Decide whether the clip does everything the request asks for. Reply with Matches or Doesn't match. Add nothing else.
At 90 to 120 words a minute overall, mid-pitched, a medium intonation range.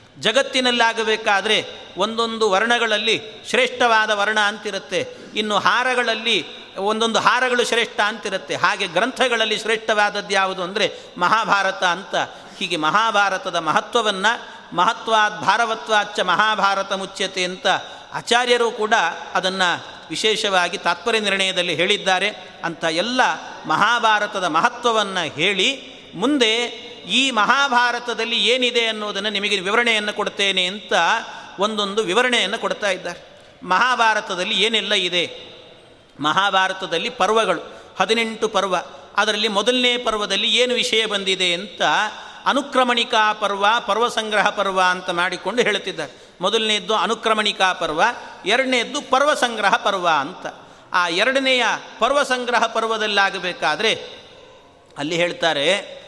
Doesn't match